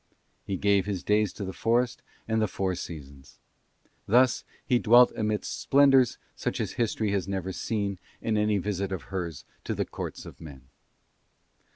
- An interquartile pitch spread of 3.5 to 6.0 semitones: No, average, 3.0 semitones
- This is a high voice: No, low, 100 Hz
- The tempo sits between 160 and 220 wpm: Yes, average, 165 wpm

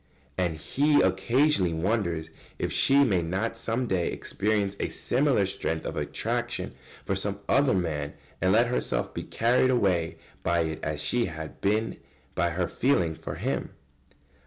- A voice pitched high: No, very low, 95 Hz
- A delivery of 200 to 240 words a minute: No, average, 155 wpm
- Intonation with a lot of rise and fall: Yes, wide, 5.8 semitones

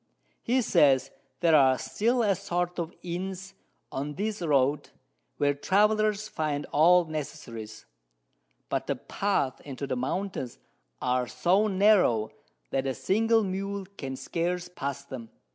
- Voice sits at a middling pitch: Yes, medium, 170 Hz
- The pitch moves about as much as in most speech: No, wide, 6.3 semitones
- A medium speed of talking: No, slow, 130 wpm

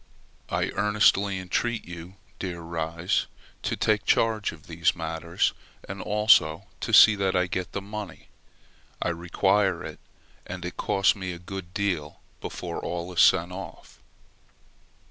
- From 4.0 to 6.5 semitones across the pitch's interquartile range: No, average, 2.7 semitones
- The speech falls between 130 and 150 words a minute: Yes, average, 145 wpm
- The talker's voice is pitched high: No, very low, 90 Hz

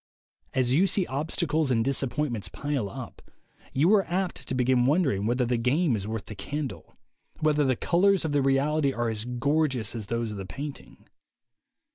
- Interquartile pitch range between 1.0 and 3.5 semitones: No, average, 4.5 semitones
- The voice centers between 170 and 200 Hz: No, low, 135 Hz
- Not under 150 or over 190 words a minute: Yes, average, 175 wpm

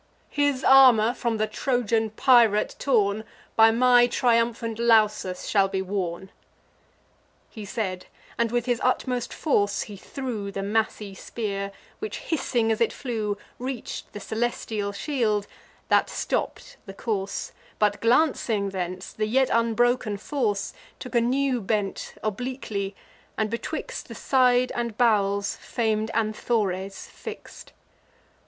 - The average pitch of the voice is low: No, high, 225 Hz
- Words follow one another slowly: Yes, slow, 125 wpm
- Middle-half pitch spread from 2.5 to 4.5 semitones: Yes, average, 3.2 semitones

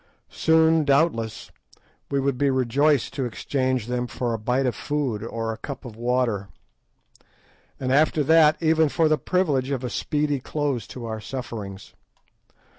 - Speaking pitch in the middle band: No, low, 130 Hz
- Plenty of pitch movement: No, average, 3.9 semitones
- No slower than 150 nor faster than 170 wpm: Yes, average, 155 wpm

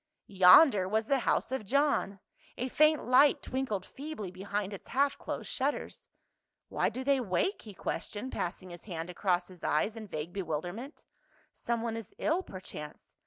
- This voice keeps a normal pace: Yes, average, 170 wpm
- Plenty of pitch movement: Yes, wide, 6.4 semitones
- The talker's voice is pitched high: Yes, high, 215 Hz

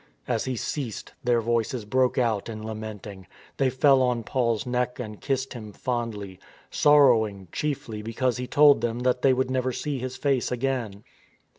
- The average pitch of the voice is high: No, low, 125 Hz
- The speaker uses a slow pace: No, average, 165 wpm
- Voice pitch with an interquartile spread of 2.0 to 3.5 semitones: Yes, average, 2.9 semitones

